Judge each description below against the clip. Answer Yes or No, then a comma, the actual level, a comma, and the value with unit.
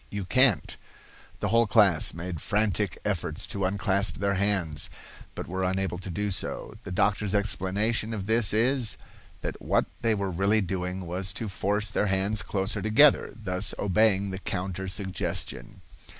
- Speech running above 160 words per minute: No, average, 155 wpm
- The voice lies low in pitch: Yes, low, 100 Hz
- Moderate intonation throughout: No, narrow, 2.3 semitones